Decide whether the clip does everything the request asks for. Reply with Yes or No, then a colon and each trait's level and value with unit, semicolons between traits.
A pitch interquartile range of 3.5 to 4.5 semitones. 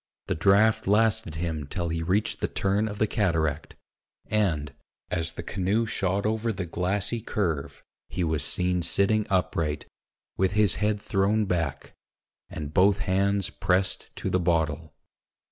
Yes: average, 3.8 semitones